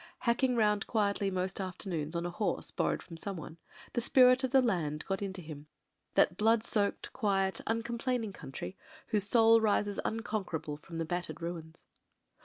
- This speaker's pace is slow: No, average, 160 wpm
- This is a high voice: Yes, high, 200 Hz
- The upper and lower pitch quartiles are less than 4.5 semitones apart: No, average, 4.8 semitones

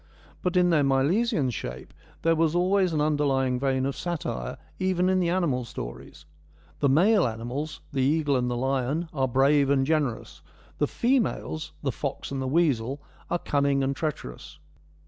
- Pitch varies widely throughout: No, average, 4.1 semitones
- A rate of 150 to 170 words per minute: Yes, average, 165 wpm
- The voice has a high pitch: No, medium, 140 Hz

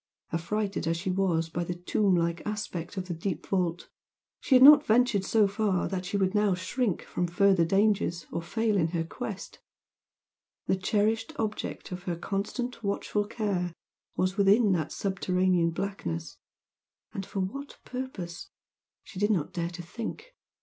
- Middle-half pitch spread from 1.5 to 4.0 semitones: Yes, average, 3.4 semitones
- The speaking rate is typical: Yes, average, 155 wpm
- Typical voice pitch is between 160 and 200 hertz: Yes, high, 190 Hz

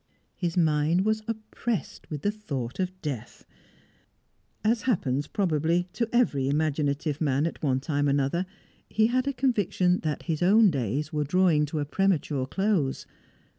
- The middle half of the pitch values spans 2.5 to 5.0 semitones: No, wide, 5.5 semitones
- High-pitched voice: No, medium, 165 Hz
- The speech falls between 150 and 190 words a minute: Yes, average, 155 wpm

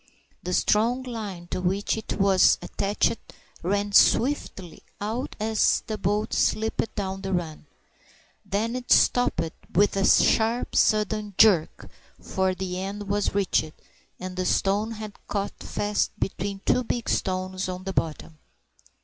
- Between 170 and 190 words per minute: No, average, 140 wpm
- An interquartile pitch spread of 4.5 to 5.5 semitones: No, narrow, 2.6 semitones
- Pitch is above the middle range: Yes, high, 200 Hz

